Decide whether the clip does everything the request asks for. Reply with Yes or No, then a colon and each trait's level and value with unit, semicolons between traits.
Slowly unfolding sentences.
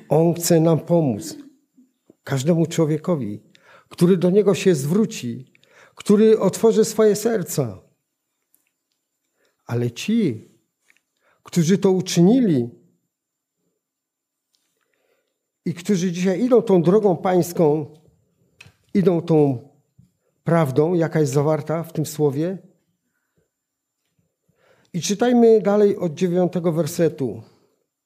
Yes: slow, 90 wpm